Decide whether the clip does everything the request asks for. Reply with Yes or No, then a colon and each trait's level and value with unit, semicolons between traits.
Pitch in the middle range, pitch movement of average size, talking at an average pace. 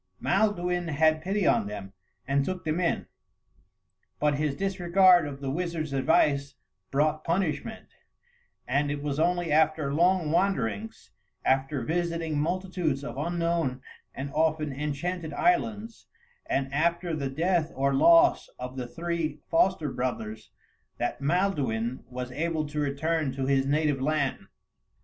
No: medium, 155 Hz; average, 3.9 semitones; slow, 130 wpm